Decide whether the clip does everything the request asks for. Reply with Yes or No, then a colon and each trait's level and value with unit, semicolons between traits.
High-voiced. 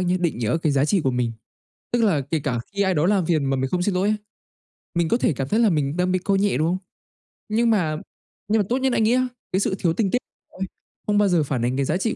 No: medium, 180 Hz